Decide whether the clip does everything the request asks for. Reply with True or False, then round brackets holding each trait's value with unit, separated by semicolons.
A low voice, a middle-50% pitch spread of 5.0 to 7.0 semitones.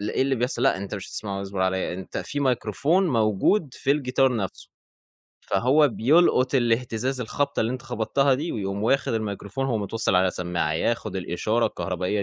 True (115 Hz; 5.3 semitones)